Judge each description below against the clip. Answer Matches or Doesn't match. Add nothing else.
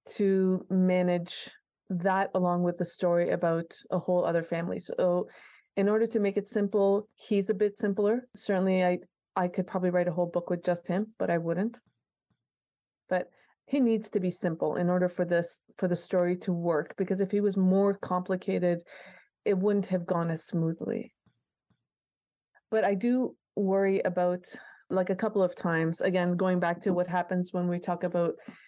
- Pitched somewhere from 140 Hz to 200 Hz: Matches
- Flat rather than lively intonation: Matches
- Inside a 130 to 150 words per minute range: Doesn't match